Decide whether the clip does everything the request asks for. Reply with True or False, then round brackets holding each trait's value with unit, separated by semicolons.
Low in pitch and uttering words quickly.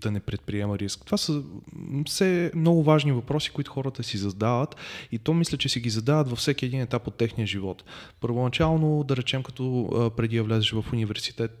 True (125 Hz; 190 wpm)